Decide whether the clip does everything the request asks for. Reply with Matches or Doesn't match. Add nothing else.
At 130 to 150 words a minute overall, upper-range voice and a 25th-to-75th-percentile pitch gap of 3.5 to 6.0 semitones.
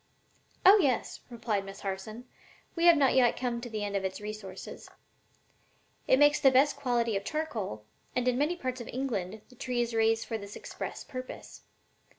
Doesn't match